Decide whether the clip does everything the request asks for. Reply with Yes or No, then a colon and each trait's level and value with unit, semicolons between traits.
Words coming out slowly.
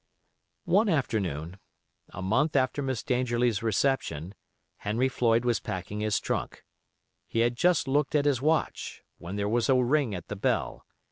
No: average, 155 wpm